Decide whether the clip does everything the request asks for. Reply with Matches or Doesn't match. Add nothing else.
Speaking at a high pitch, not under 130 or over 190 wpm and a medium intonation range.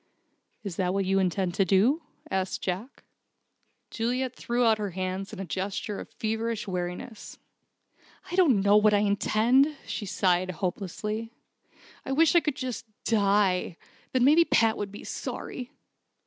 Matches